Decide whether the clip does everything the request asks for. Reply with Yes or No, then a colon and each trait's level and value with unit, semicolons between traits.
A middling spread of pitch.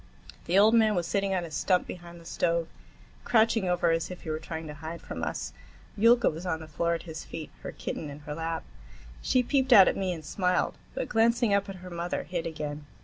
Yes: average, 3.6 semitones